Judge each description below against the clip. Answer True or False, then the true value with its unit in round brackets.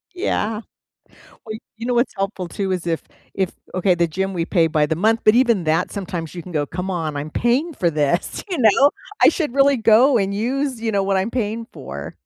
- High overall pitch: True (195 Hz)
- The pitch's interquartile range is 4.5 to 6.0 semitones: True (5.2 semitones)